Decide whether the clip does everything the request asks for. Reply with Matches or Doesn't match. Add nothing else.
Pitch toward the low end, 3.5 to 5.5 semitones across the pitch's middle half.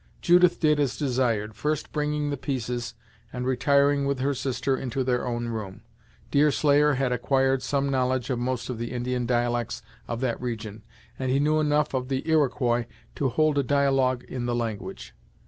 Doesn't match